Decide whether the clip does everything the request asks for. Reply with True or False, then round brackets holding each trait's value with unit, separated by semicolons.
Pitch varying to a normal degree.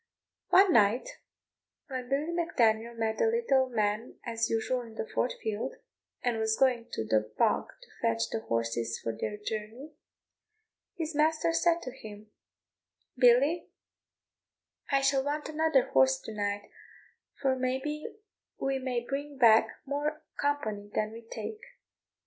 True (5.0 semitones)